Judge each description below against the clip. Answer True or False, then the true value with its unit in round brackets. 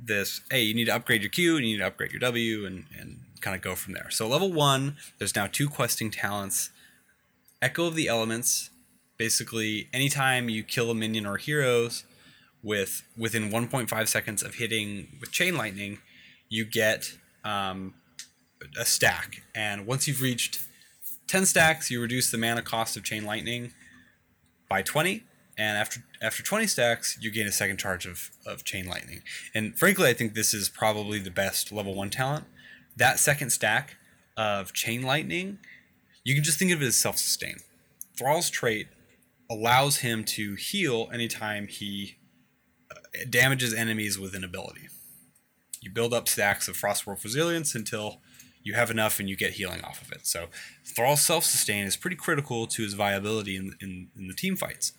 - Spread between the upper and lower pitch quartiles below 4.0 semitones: True (3.6 semitones)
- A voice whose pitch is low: True (110 Hz)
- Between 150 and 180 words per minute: True (175 wpm)